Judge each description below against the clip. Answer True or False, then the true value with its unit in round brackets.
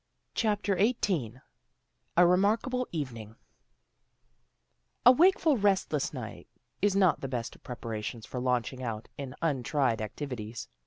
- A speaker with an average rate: False (115 wpm)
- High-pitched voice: False (140 Hz)